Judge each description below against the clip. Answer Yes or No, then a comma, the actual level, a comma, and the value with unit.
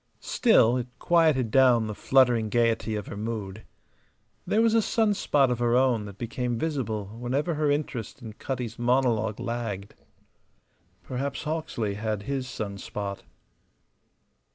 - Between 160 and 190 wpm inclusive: No, average, 140 wpm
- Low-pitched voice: Yes, low, 120 Hz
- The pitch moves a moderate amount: Yes, average, 3.8 semitones